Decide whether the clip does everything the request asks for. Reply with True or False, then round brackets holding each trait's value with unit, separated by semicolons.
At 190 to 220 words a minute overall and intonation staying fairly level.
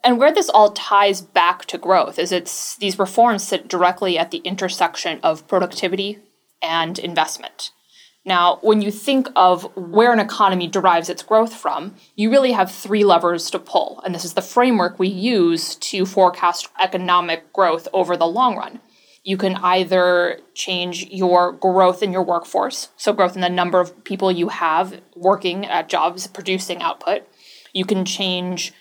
False (170 wpm; 2.1 semitones)